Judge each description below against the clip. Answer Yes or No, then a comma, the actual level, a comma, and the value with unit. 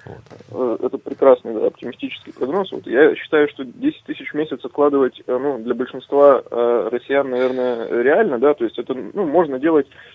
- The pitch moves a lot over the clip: Yes, wide, 6.1 semitones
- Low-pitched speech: No, medium, 145 Hz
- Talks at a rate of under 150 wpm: No, fast, 160 wpm